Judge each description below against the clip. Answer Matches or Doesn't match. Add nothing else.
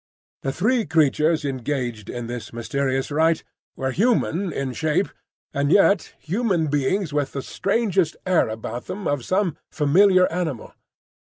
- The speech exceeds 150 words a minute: Doesn't match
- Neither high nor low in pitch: Matches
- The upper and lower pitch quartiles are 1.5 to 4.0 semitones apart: Doesn't match